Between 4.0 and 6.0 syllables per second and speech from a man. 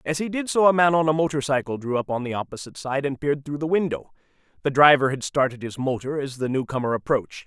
No: 6.6 syllables/s; male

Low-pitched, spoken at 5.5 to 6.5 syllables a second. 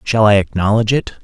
Yes: low, 110 Hz; 6.3 syllables/s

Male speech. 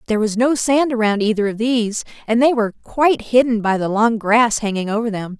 No: female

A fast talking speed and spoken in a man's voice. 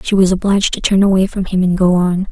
No: fast, 285 wpm; female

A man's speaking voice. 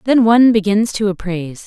No: female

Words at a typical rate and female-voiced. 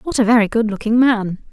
No: fast, 235 wpm; female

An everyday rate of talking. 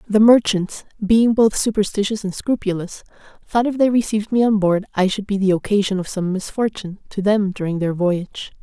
Yes: average, 190 wpm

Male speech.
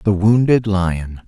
Yes: male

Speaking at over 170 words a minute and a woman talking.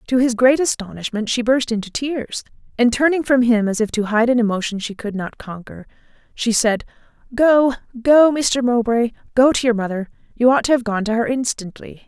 Yes: average, 190 wpm; female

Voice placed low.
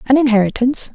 No: high, 245 Hz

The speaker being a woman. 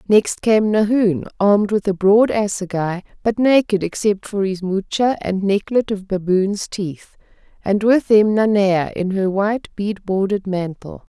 Yes: female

